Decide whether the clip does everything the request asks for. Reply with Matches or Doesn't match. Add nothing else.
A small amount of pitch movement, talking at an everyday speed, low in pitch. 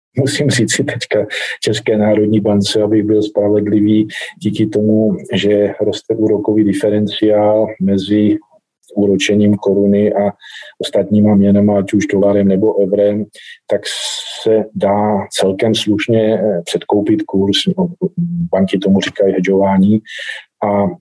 Doesn't match